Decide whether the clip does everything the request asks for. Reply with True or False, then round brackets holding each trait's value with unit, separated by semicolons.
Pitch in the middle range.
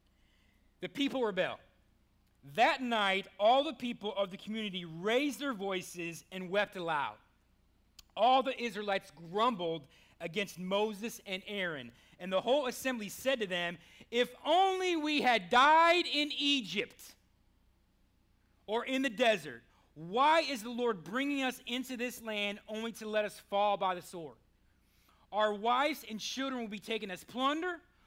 False (210 Hz)